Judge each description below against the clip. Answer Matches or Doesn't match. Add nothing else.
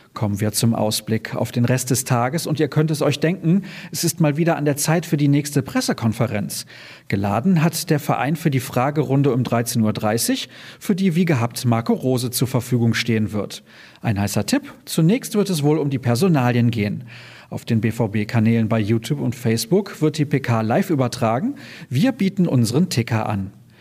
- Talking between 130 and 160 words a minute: Doesn't match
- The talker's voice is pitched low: Matches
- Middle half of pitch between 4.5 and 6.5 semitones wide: Matches